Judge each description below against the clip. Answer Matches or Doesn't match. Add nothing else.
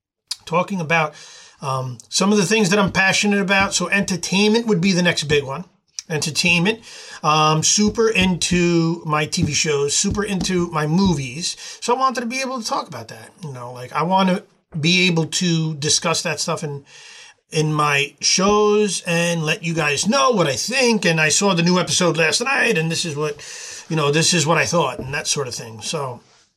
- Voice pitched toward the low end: Doesn't match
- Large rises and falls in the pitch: Doesn't match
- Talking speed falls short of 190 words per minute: Doesn't match